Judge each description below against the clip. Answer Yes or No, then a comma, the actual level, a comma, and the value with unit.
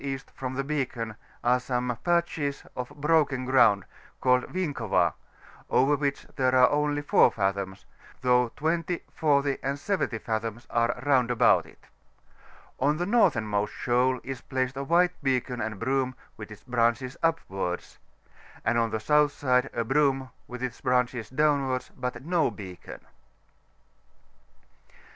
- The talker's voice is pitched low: Yes, low, 130 Hz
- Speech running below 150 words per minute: Yes, slow, 135 wpm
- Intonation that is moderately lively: Yes, average, 3.4 semitones